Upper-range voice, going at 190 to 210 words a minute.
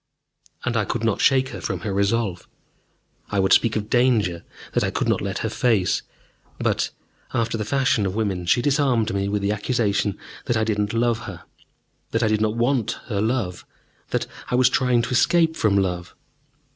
No: low, 110 Hz; average, 195 wpm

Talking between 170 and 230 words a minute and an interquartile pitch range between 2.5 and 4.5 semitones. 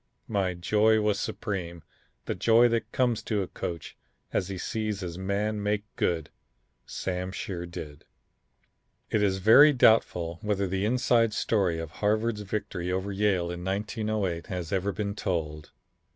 No: average, 150 wpm; average, 3.4 semitones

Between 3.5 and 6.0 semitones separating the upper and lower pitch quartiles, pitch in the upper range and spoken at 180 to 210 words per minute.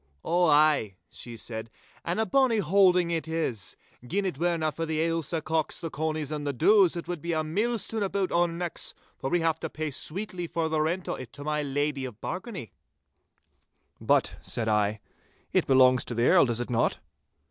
No: average, 4.6 semitones; medium, 160 Hz; average, 195 wpm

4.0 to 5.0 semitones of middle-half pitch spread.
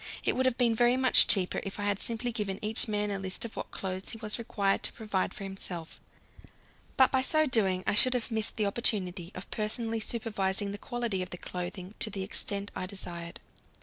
No: average, 3.2 semitones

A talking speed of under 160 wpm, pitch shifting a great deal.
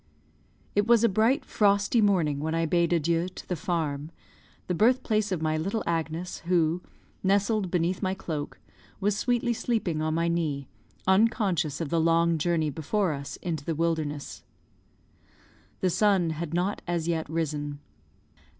No: average, 150 wpm; average, 3.8 semitones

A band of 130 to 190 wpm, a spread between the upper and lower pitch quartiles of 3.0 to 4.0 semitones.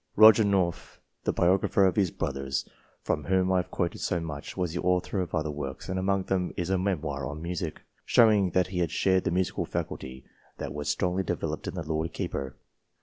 No: average, 200 wpm; average, 3.4 semitones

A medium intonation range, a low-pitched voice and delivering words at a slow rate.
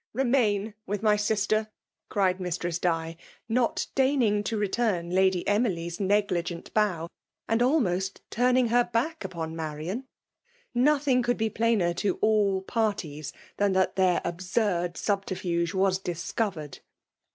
No: average, 4.3 semitones; high, 200 Hz; slow, 130 wpm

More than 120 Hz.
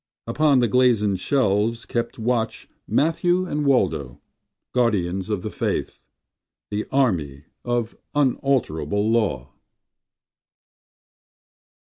No: low, 115 Hz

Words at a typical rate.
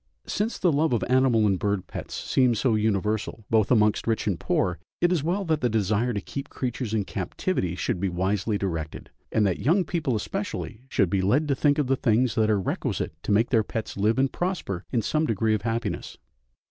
No: fast, 210 wpm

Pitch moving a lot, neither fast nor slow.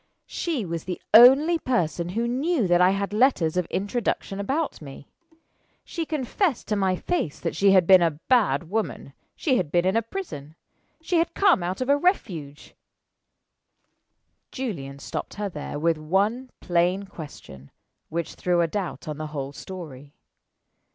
Yes: wide, 7.2 semitones; average, 165 wpm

